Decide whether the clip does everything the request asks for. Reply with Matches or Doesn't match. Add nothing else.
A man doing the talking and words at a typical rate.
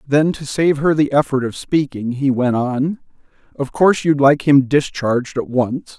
Matches